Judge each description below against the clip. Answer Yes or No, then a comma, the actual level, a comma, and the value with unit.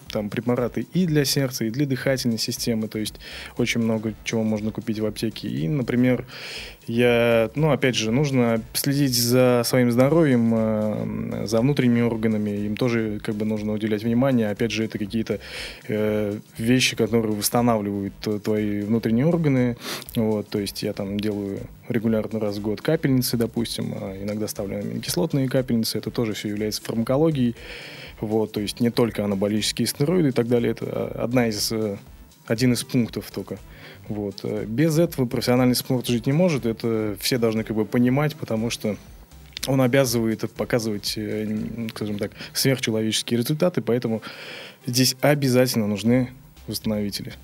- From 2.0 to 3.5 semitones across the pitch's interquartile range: Yes, average, 2.8 semitones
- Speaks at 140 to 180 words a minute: Yes, average, 150 wpm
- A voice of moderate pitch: No, low, 115 Hz